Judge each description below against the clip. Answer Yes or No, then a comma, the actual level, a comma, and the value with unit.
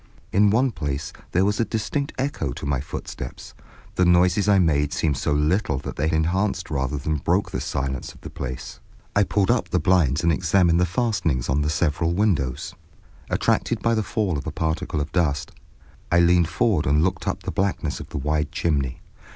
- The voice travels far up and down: No, average, 4.7 semitones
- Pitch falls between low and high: No, very low, 85 Hz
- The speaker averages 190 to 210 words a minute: Yes, average, 195 wpm